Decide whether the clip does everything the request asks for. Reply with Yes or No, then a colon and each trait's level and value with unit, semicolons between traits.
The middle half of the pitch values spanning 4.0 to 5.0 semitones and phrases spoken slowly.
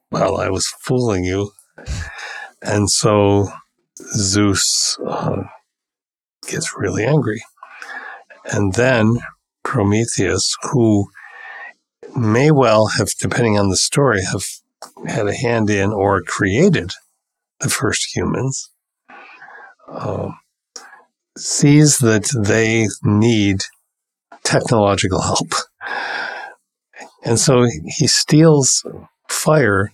No: average, 3.3 semitones; slow, 90 wpm